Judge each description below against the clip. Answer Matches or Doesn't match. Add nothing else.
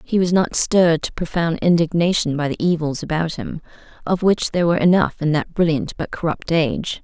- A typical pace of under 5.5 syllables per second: Doesn't match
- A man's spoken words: Doesn't match